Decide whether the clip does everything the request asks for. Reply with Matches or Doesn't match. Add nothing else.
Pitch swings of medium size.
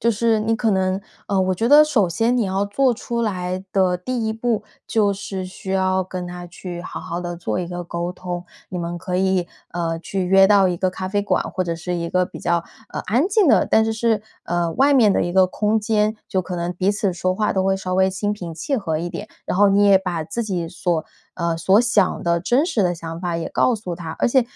Matches